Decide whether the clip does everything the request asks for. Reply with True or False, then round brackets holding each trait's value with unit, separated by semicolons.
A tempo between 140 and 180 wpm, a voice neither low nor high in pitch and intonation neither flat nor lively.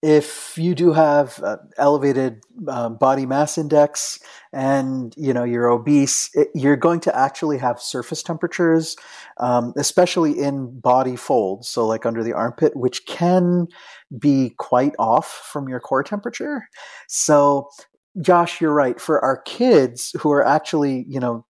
True (150 wpm; 145 Hz; 4.5 semitones)